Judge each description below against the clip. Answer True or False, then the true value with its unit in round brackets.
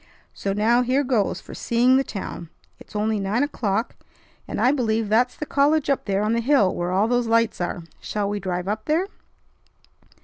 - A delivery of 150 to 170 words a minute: False (195 wpm)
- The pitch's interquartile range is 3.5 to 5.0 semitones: True (4.0 semitones)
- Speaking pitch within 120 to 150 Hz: False (225 Hz)